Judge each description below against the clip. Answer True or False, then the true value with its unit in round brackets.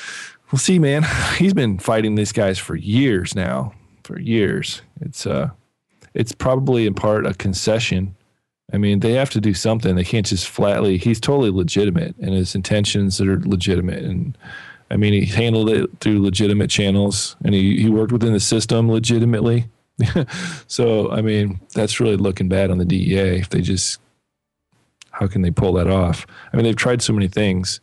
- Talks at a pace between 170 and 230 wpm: True (180 wpm)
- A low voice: True (105 Hz)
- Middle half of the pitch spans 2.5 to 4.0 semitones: True (3.1 semitones)